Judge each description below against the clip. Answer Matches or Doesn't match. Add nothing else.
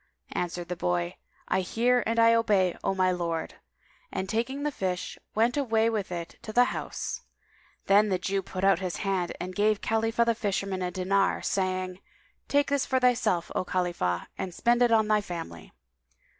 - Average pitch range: Matches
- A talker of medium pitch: Doesn't match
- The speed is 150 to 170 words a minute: Doesn't match